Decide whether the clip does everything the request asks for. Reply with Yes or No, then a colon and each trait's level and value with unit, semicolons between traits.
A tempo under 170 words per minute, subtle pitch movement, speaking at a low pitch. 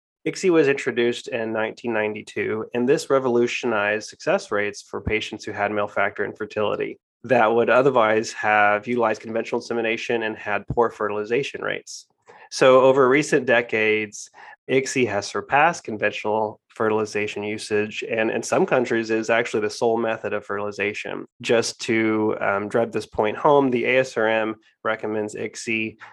Yes: average, 140 wpm; narrow, 2.0 semitones; low, 110 Hz